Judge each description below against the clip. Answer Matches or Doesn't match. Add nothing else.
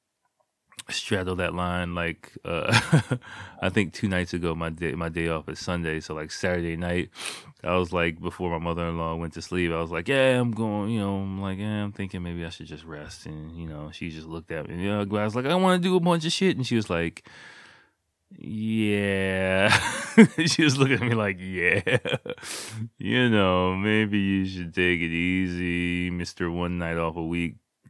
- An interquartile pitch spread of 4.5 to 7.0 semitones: Doesn't match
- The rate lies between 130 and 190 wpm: Doesn't match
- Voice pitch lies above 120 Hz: Doesn't match